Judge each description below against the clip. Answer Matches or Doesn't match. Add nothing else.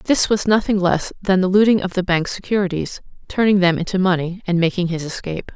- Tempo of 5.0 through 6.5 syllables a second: Matches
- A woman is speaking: Matches